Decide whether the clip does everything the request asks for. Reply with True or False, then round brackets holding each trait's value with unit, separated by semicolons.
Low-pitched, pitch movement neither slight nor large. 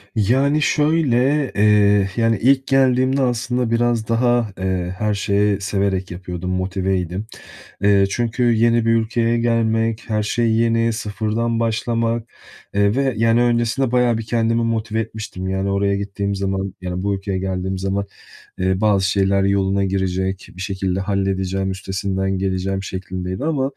True (105 Hz; 3.3 semitones)